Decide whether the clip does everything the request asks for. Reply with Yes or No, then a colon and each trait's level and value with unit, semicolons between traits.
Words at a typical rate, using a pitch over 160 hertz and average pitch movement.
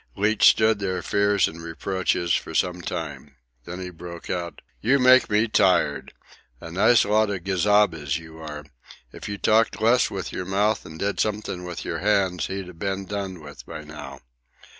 No: average, 180 wpm; very low, 95 Hz; average, 3.6 semitones